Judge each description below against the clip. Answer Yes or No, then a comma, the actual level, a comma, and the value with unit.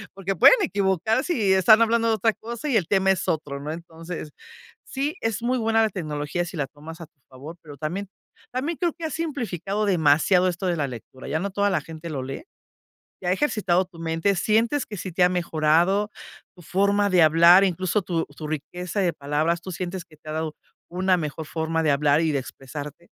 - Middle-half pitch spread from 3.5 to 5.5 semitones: Yes, average, 4.4 semitones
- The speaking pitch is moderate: Yes, medium, 180 Hz